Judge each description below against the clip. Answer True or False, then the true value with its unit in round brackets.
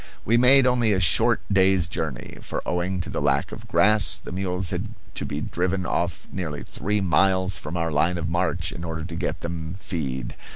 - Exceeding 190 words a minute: True (200 wpm)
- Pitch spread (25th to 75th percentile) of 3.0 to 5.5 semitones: False (2.5 semitones)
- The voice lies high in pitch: False (90 Hz)